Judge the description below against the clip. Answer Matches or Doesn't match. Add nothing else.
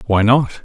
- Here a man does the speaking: Matches